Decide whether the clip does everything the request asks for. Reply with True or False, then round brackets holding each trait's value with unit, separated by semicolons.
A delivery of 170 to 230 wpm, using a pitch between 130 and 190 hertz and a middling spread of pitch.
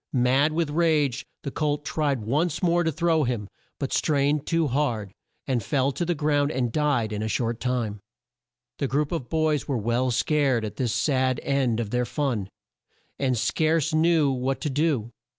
True (180 wpm; 140 Hz; 3.8 semitones)